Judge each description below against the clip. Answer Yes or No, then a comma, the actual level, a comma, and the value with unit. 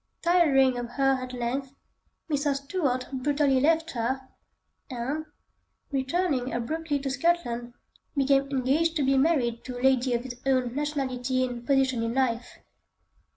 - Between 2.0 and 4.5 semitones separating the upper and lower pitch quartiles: Yes, narrow, 2.5 semitones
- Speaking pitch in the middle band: No, very high, 265 Hz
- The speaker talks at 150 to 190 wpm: No, average, 140 wpm